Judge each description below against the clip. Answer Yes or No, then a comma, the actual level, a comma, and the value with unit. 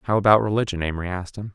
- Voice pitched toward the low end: Yes, low, 100 Hz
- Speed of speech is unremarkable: No, fast, 230 wpm